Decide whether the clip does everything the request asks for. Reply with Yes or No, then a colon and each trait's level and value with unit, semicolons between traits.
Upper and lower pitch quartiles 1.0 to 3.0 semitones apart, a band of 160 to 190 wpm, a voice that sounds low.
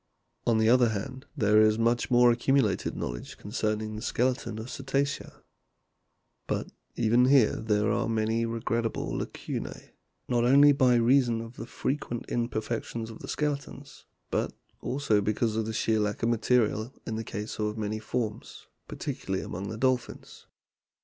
Yes: narrow, 2.5 semitones; average, 165 wpm; low, 115 Hz